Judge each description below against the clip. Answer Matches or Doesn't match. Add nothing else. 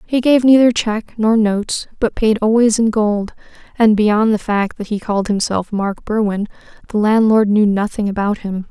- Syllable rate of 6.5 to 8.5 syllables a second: Doesn't match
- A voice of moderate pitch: Doesn't match